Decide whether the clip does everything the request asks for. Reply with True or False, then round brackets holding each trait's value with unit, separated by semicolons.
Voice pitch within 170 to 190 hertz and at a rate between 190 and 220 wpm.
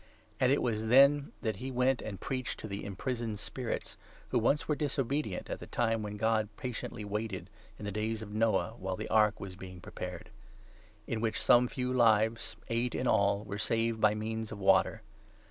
False (110 Hz; 195 wpm)